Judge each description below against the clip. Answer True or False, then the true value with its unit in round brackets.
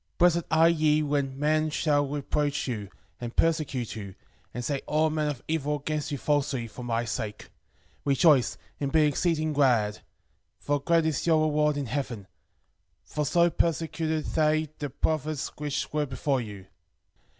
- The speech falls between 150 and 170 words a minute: True (160 wpm)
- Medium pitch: True (150 Hz)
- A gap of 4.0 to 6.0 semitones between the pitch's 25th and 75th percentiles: False (2.8 semitones)